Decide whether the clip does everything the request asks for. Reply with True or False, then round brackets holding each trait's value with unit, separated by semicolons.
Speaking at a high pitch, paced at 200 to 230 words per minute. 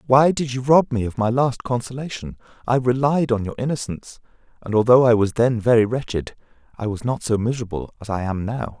False (120 Hz; 205 wpm)